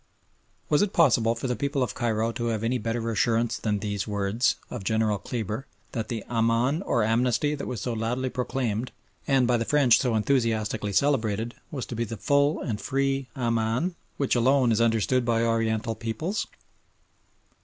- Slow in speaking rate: No, average, 175 wpm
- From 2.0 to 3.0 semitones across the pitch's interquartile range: Yes, average, 2.7 semitones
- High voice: No, low, 115 Hz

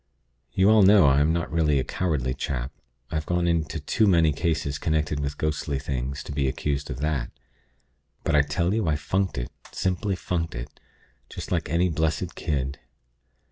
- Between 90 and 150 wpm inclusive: No, average, 180 wpm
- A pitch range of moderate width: Yes, average, 3.4 semitones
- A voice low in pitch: Yes, very low, 75 Hz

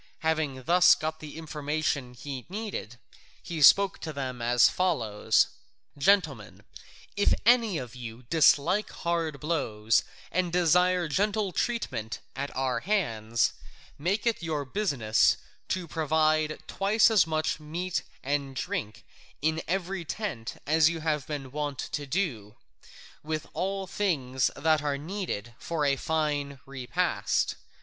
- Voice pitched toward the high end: No, medium, 155 Hz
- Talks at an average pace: No, slow, 130 wpm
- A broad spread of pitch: No, average, 5.0 semitones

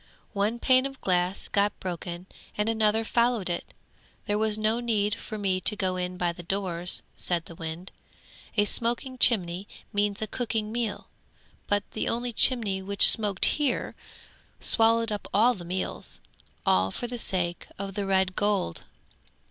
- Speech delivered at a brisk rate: No, average, 160 wpm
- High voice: Yes, high, 205 Hz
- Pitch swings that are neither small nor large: Yes, average, 3.5 semitones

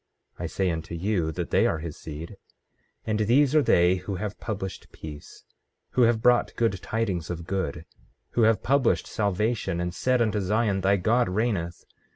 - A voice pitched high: No, low, 100 Hz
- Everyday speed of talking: Yes, average, 180 wpm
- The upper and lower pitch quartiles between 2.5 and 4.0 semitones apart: No, average, 4.6 semitones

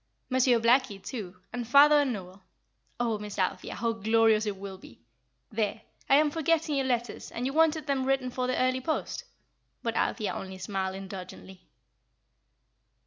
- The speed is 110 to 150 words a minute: No, average, 160 wpm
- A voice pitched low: No, high, 235 Hz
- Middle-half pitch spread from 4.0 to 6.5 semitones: Yes, average, 5.0 semitones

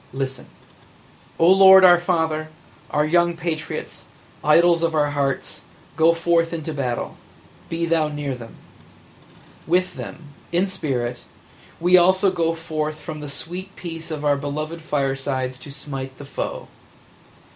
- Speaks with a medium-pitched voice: Yes, medium, 155 Hz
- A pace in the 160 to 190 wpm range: No, average, 145 wpm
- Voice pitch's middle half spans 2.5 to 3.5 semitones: Yes, average, 3.1 semitones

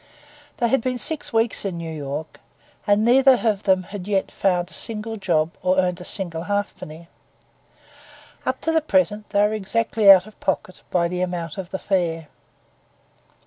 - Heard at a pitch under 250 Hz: Yes, high, 190 Hz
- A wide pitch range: No, average, 3.6 semitones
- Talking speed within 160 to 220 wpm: Yes, average, 175 wpm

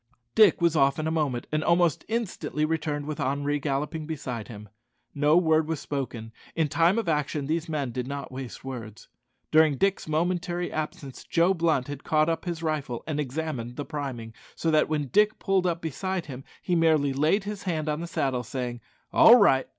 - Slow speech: No, average, 190 wpm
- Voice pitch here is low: No, medium, 155 Hz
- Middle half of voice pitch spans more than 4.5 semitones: No, average, 3.5 semitones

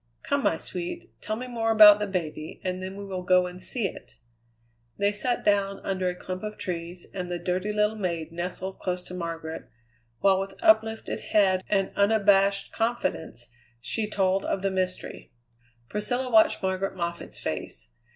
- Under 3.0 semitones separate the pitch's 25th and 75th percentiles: Yes, narrow, 2.6 semitones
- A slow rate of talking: No, average, 170 wpm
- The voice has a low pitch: No, high, 195 Hz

